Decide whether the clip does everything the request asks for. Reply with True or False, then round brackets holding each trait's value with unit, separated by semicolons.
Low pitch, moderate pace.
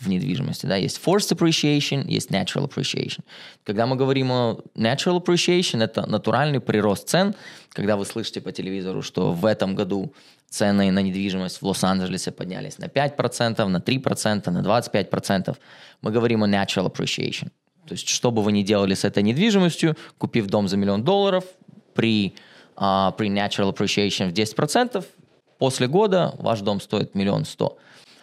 False (115 Hz; 165 wpm)